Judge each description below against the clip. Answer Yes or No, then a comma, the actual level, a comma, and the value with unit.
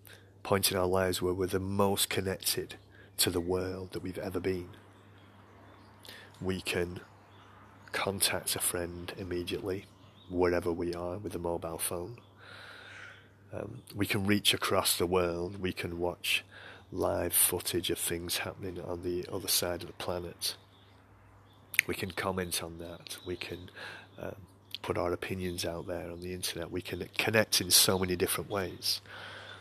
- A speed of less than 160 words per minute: Yes, average, 150 wpm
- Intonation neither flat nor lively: No, narrow, 1.9 semitones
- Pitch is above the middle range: No, very low, 95 Hz